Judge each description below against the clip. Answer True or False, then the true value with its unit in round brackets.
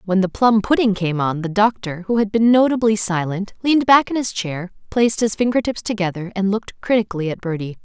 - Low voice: False (205 Hz)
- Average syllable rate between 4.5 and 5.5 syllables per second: False (5.8 syllables/s)